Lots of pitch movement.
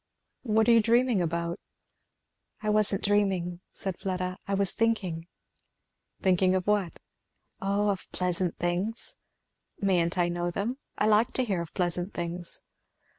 No: average, 3.1 semitones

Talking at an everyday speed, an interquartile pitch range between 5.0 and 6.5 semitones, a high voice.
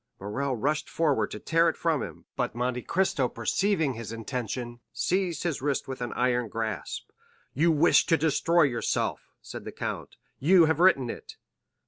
No: average, 165 wpm; average, 5.3 semitones; medium, 140 Hz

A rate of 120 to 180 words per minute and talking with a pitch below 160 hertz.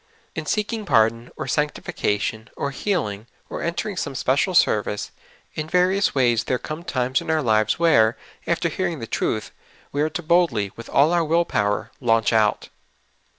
Yes: average, 165 wpm; medium, 140 Hz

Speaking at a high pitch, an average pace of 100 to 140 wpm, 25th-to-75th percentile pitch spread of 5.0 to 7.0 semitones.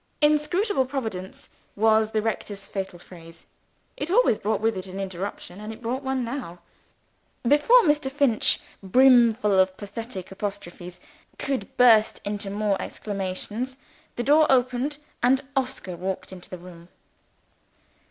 Yes: high, 220 Hz; slow, 135 wpm; wide, 5.5 semitones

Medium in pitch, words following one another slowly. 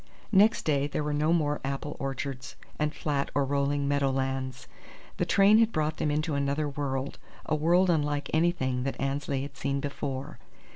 No: medium, 145 Hz; average, 175 wpm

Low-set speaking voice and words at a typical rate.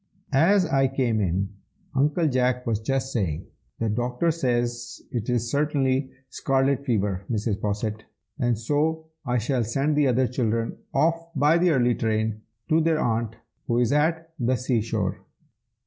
Yes: low, 125 Hz; average, 150 wpm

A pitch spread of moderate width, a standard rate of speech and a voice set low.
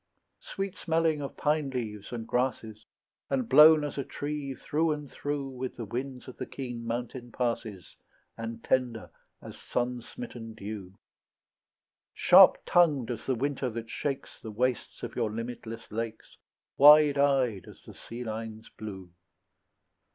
Yes: average, 4.0 semitones; average, 145 wpm; low, 125 Hz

